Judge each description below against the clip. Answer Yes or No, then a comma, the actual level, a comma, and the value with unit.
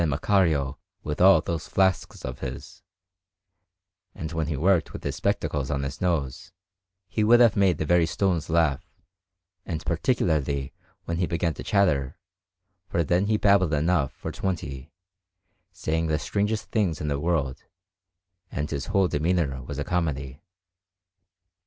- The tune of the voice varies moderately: Yes, average, 4.2 semitones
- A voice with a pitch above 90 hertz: No, very low, 80 Hz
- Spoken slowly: No, average, 145 wpm